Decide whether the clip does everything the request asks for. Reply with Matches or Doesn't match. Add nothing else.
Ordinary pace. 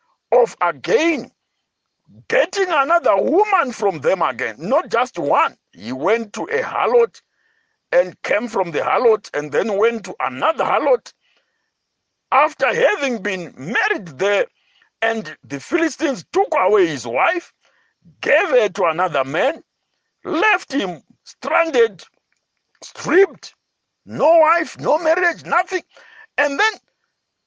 Doesn't match